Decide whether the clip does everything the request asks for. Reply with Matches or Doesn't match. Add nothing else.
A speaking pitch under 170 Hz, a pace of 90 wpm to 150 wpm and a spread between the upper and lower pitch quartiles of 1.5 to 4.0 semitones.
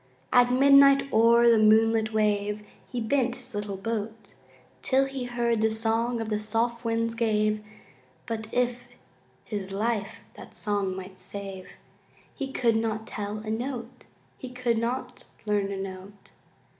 Doesn't match